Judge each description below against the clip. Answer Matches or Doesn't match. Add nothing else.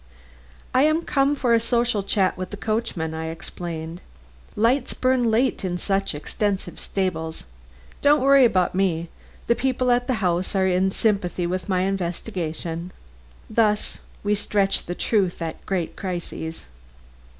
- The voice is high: Matches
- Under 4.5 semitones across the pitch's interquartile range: Doesn't match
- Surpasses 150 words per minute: Doesn't match